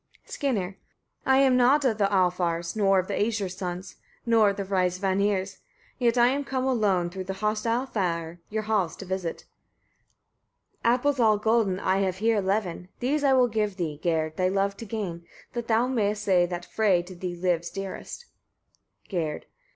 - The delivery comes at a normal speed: Yes, average, 180 wpm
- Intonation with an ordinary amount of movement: Yes, average, 3.9 semitones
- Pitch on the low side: No, high, 200 Hz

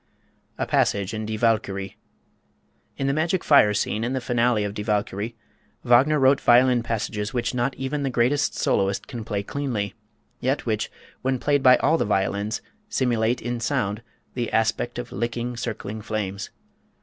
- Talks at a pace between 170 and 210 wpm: No, average, 160 wpm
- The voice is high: No, low, 120 Hz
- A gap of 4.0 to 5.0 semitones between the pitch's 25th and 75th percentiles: No, average, 3.6 semitones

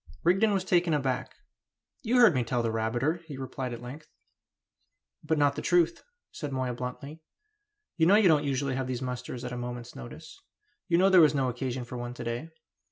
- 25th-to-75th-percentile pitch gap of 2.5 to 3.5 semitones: No, average, 4.8 semitones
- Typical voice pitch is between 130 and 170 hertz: Yes, low, 135 Hz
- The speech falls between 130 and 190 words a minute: No, average, 200 wpm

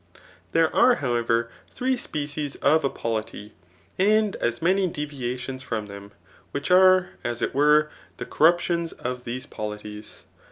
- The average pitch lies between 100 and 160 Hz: Yes, medium, 140 Hz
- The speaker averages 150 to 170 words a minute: No, slow, 135 wpm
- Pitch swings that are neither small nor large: No, wide, 6.4 semitones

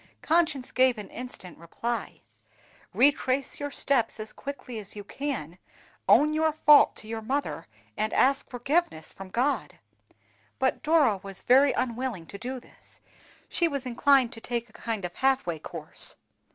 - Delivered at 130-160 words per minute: Yes, average, 155 wpm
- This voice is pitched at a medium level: No, very high, 255 Hz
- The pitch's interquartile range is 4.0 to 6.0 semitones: Yes, average, 4.5 semitones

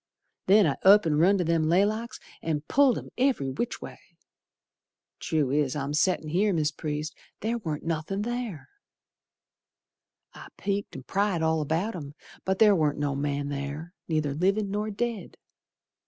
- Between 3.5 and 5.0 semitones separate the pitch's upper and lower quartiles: No, wide, 5.5 semitones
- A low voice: No, medium, 165 Hz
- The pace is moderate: Yes, average, 155 wpm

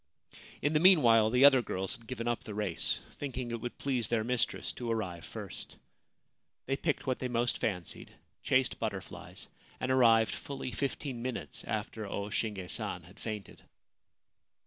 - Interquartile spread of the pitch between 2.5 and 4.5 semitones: Yes, average, 3.1 semitones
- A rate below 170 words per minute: Yes, average, 160 wpm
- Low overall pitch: Yes, low, 120 Hz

